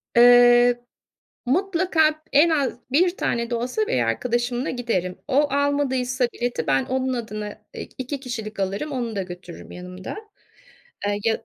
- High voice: Yes, high, 245 Hz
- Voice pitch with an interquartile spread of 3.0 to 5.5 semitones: Yes, average, 4.3 semitones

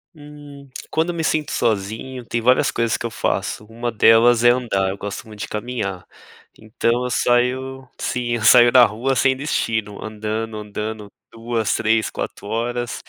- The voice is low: Yes, low, 115 Hz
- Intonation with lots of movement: No, narrow, 2.5 semitones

